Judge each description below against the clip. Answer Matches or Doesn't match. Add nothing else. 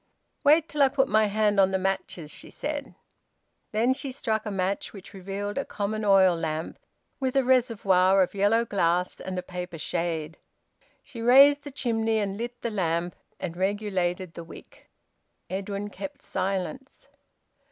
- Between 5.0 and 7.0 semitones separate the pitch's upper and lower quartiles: Doesn't match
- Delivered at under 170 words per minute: Matches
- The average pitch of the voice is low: Doesn't match